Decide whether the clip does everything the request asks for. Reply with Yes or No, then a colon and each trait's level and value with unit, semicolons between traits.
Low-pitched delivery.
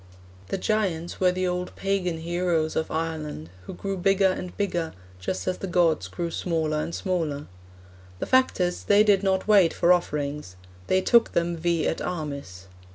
No: medium, 175 Hz